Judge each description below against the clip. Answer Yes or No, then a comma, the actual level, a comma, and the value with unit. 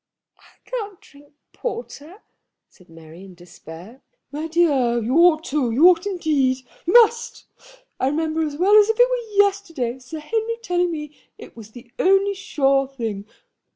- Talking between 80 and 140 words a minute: No, average, 160 wpm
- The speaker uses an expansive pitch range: Yes, wide, 7.4 semitones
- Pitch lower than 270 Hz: No, very high, 310 Hz